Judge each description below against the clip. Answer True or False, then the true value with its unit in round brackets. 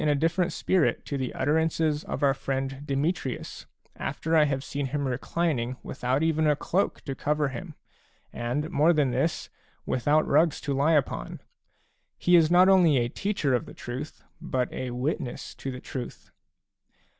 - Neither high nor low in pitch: True (145 Hz)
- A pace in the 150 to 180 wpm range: True (170 wpm)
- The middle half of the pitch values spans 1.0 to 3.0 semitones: False (3.4 semitones)